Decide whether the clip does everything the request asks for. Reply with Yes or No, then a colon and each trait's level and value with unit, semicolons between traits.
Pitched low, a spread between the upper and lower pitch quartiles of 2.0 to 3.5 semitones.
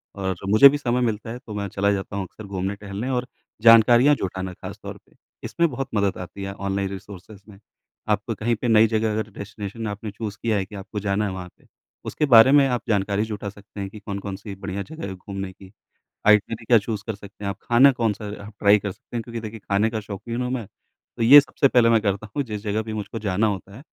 Yes: low, 105 Hz; narrow, 2.6 semitones